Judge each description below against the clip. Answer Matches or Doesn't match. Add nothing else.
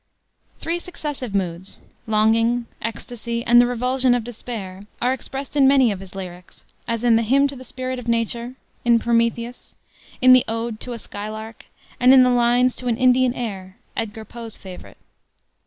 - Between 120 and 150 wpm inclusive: Doesn't match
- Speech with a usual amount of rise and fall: Doesn't match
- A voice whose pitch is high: Matches